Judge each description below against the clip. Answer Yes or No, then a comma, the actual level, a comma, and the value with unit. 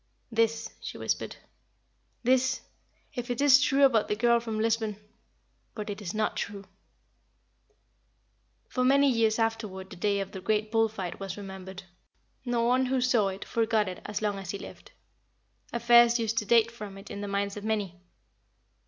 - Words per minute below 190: Yes, average, 170 wpm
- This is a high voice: Yes, high, 220 Hz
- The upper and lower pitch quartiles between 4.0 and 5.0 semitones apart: No, average, 2.8 semitones